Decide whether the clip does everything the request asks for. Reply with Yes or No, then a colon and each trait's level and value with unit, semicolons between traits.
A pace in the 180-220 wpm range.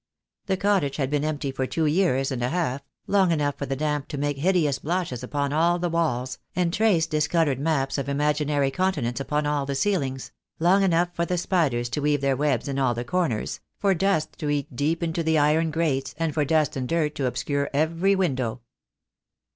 Yes: average, 200 wpm